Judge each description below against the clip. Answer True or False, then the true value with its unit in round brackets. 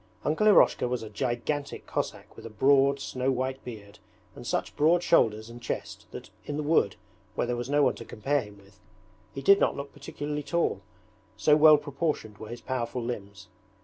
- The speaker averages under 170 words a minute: False (190 wpm)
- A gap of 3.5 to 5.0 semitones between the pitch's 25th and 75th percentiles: True (4.5 semitones)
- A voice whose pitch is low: True (130 Hz)